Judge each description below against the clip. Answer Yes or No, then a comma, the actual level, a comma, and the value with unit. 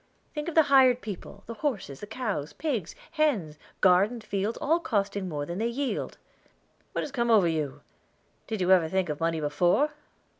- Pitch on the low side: No, high, 205 Hz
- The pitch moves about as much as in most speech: No, wide, 6.9 semitones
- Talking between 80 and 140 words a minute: No, average, 180 wpm